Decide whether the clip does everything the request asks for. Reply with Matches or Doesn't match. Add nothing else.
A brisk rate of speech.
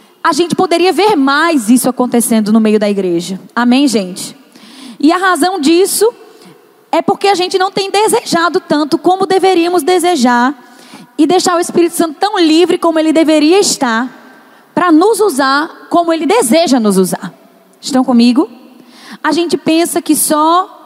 Doesn't match